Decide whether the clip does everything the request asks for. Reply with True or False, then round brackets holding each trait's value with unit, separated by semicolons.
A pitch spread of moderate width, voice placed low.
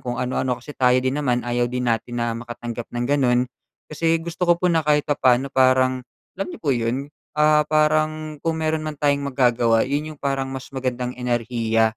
True (3.8 semitones; 130 Hz)